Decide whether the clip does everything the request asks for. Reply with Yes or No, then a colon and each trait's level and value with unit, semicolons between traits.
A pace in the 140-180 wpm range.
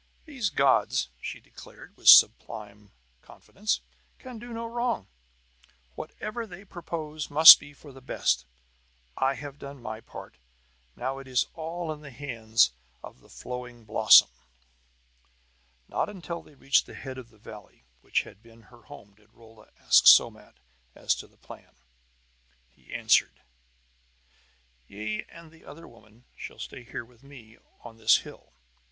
Yes: average, 150 wpm